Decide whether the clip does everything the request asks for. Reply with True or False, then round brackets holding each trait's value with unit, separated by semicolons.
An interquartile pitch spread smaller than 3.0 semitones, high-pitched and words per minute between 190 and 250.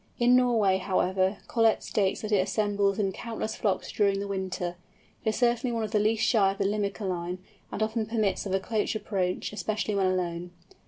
True (2.5 semitones; 205 Hz; 195 wpm)